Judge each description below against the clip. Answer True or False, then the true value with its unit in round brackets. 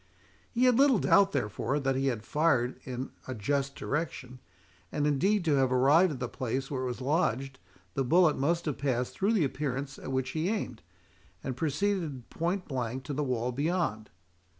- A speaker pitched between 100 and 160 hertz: True (140 Hz)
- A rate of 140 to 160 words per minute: False (185 wpm)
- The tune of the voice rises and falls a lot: False (4.5 semitones)